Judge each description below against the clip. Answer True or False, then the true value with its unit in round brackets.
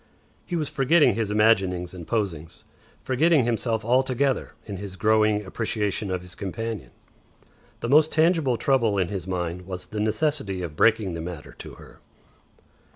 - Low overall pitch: True (110 Hz)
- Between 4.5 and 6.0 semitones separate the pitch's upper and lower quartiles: True (5.6 semitones)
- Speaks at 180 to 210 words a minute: False (155 wpm)